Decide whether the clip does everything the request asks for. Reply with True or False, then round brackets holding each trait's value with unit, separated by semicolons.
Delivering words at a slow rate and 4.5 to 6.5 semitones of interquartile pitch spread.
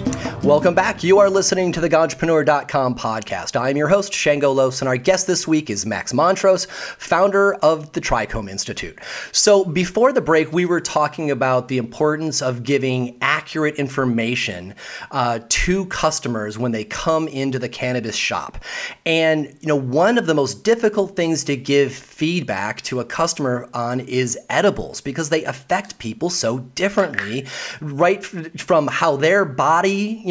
False (160 wpm; 5.5 semitones)